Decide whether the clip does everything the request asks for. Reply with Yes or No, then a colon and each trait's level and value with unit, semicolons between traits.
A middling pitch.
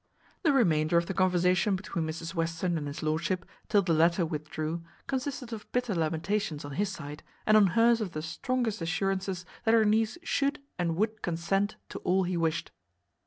Yes: medium, 180 Hz